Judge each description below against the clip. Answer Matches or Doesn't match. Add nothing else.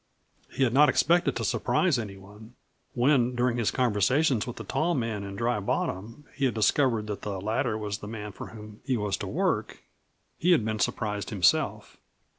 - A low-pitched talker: Matches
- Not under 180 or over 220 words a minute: Matches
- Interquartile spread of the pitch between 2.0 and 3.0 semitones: Doesn't match